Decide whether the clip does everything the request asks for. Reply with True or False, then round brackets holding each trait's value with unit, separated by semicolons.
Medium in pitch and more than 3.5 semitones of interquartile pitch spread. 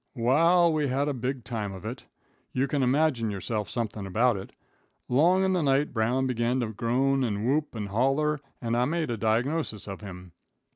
False (125 Hz; 4.4 semitones)